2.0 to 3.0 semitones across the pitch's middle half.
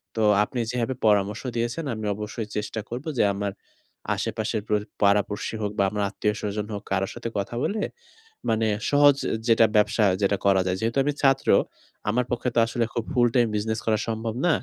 Yes: narrow, 2.4 semitones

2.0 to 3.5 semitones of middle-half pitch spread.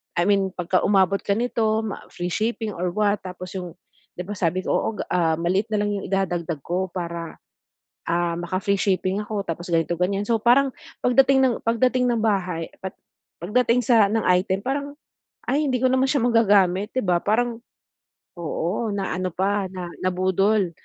No: average, 3.9 semitones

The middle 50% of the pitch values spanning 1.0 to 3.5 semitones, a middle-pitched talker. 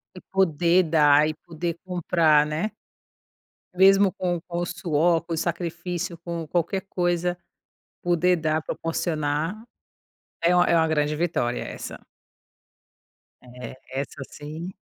Yes: narrow, 2.4 semitones; medium, 170 Hz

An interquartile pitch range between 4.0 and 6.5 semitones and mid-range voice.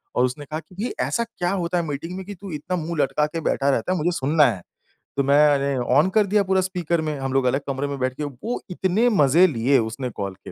Yes: average, 5.0 semitones; medium, 150 Hz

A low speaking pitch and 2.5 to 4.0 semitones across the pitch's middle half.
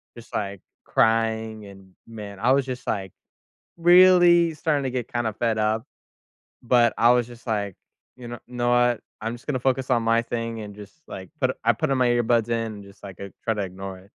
Yes: low, 115 Hz; average, 2.9 semitones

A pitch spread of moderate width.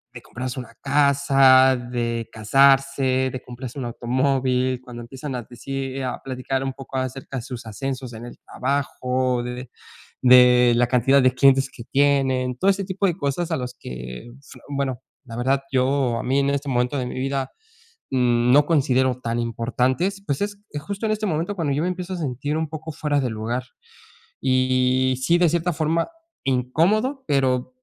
No: narrow, 2.2 semitones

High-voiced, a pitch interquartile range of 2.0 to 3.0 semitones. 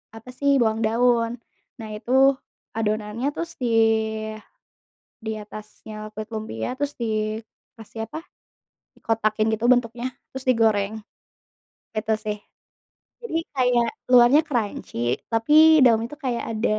Yes: high, 225 Hz; narrow, 2.5 semitones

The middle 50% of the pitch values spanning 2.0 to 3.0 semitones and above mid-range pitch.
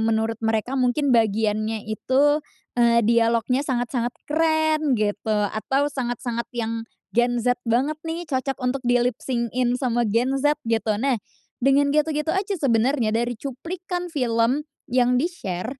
No: average, 3.7 semitones; high, 245 Hz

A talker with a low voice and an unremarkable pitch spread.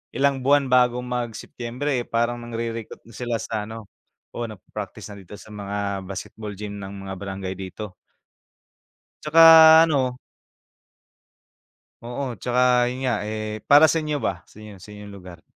Yes: low, 115 Hz; average, 3.7 semitones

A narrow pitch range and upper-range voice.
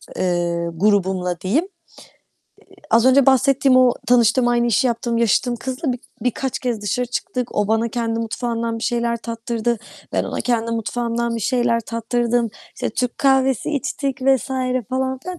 Yes: narrow, 2.1 semitones; high, 235 Hz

